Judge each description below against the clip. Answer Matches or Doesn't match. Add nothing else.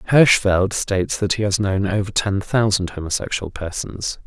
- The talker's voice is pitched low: Matches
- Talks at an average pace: Matches